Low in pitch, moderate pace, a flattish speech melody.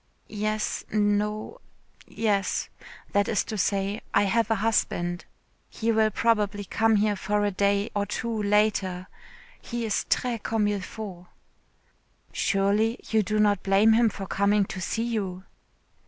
No: high, 210 Hz; average, 145 wpm; narrow, 1.7 semitones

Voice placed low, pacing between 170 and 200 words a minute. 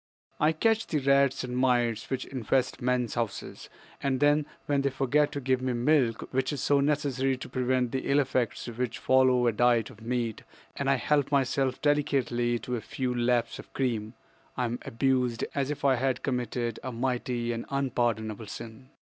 Yes: low, 130 Hz; average, 180 wpm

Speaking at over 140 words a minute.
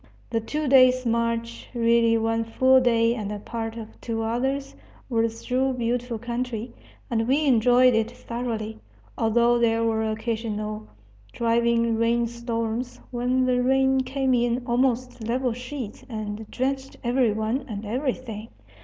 No: slow, 135 wpm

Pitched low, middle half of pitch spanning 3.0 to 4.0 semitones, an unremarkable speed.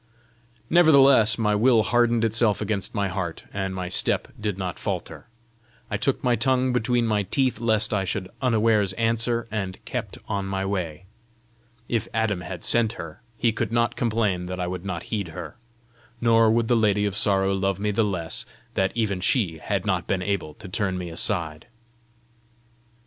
Yes: low, 105 Hz; average, 3.5 semitones; average, 175 wpm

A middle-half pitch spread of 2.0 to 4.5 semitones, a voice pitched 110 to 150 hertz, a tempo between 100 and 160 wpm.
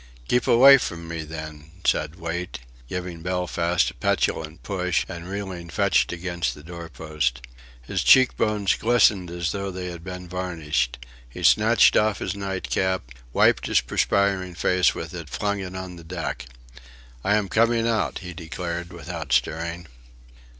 No: average, 2.8 semitones; very low, 90 Hz; average, 150 wpm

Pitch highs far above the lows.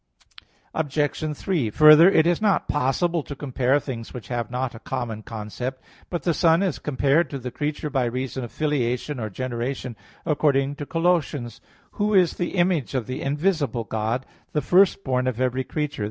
No: average, 4.1 semitones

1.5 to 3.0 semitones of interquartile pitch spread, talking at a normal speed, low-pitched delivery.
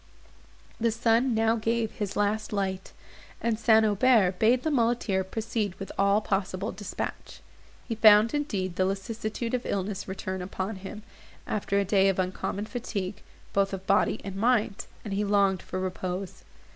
No: average, 2.7 semitones; average, 160 wpm; high, 205 Hz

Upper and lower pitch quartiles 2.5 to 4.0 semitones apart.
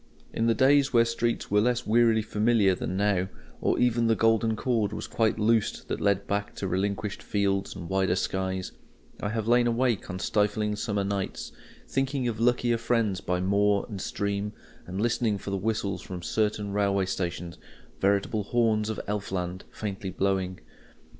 Yes: average, 2.9 semitones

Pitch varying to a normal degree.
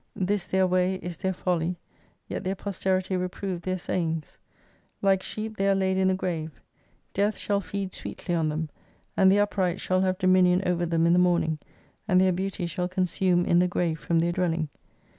No: narrow, 1.6 semitones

